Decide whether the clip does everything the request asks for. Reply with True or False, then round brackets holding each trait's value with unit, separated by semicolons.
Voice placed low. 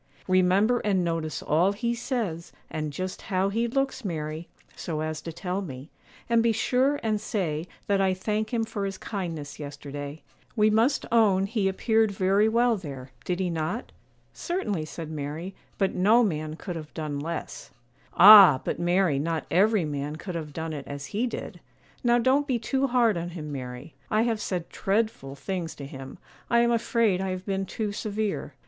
False (190 Hz)